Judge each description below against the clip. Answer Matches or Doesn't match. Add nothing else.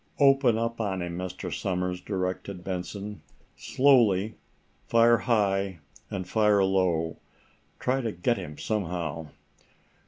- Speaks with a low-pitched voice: Matches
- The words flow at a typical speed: Doesn't match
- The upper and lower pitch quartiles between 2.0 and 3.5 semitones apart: Doesn't match